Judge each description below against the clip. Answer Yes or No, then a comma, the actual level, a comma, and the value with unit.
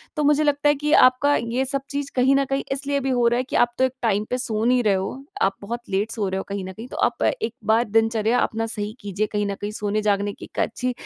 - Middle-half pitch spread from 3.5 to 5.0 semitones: Yes, average, 4.2 semitones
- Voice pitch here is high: Yes, high, 235 Hz